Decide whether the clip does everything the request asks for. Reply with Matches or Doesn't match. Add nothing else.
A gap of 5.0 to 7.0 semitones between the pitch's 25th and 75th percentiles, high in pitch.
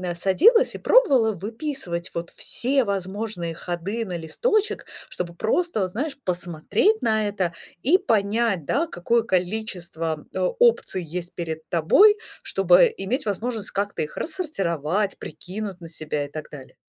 Matches